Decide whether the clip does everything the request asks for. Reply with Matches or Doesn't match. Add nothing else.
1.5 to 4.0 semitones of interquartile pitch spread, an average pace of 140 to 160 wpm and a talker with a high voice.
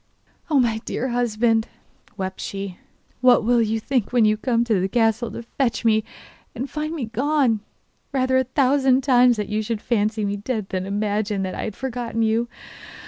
Doesn't match